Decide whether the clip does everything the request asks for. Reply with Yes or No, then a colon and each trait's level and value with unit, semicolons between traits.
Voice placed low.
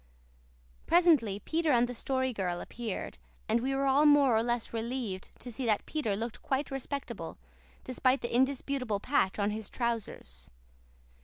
No: high, 245 Hz